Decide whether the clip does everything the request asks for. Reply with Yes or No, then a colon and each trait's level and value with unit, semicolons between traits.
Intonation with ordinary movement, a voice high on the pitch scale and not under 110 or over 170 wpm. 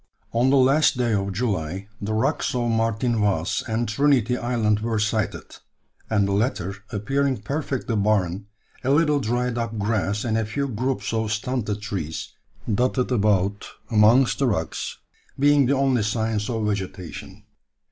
No: average, 3.4 semitones; low, 110 Hz; average, 150 wpm